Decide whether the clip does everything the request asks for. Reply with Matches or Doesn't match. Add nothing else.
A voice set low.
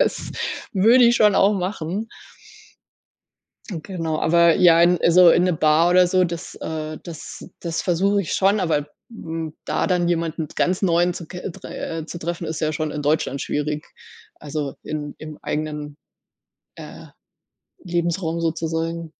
Doesn't match